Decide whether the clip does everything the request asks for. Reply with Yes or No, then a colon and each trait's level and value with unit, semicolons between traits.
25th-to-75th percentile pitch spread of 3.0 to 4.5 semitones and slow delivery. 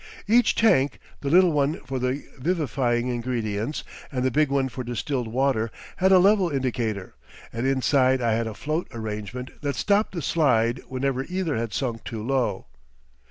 No: average, 4.1 semitones; average, 165 wpm